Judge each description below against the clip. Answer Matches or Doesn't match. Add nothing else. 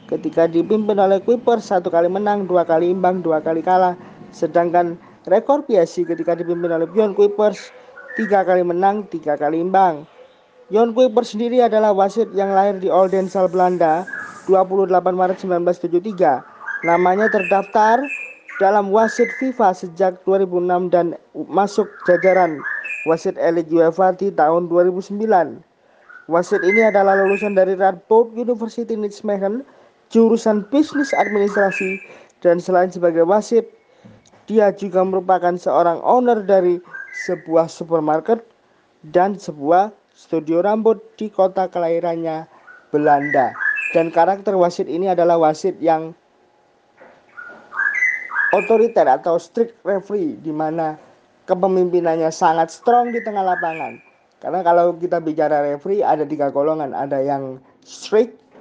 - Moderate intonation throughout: Matches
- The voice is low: Doesn't match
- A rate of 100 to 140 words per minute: Matches